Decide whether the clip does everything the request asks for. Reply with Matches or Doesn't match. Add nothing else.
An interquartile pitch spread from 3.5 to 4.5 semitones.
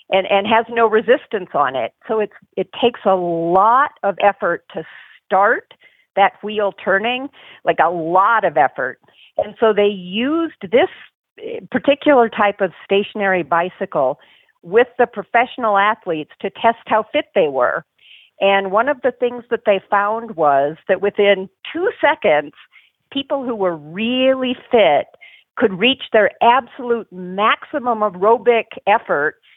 Matches